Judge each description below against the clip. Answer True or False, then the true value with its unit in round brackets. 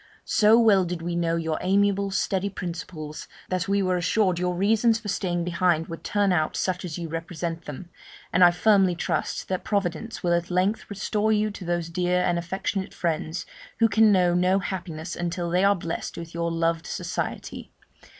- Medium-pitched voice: True (180 Hz)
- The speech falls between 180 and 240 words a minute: True (185 wpm)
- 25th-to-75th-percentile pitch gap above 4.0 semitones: False (2.8 semitones)